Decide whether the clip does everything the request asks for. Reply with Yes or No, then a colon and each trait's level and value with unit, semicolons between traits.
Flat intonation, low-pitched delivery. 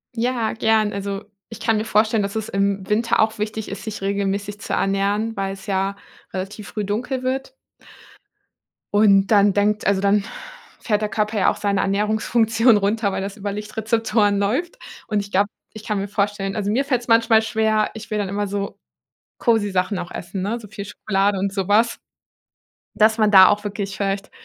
No: narrow, 1.8 semitones; high, 205 Hz